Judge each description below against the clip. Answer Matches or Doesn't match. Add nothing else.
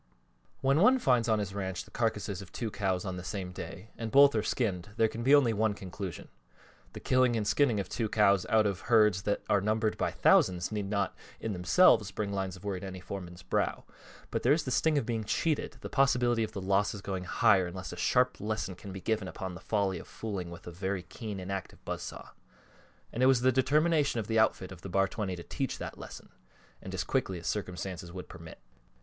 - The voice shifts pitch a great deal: Doesn't match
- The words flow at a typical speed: Doesn't match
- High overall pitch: Doesn't match